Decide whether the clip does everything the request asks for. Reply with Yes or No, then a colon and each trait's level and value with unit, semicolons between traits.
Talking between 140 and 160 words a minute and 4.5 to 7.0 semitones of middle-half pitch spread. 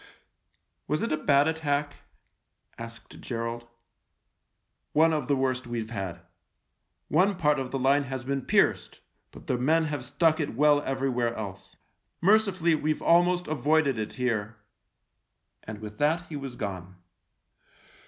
Yes: average, 155 wpm; average, 4.8 semitones